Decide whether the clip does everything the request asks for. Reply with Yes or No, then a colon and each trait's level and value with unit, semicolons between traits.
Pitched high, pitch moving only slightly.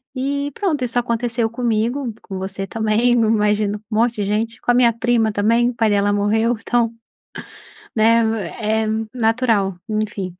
Yes: high, 225 Hz; narrow, 2.3 semitones